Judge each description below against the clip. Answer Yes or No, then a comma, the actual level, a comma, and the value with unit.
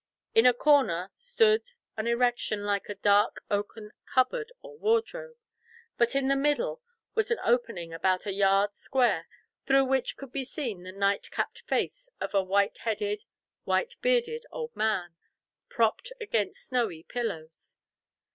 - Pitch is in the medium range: No, high, 245 Hz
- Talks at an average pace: Yes, average, 145 wpm